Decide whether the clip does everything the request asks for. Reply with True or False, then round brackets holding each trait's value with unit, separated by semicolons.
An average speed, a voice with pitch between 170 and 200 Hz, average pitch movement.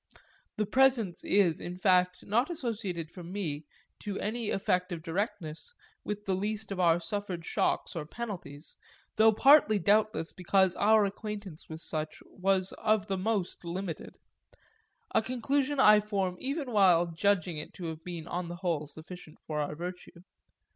True (155 wpm; 190 Hz; 3.9 semitones)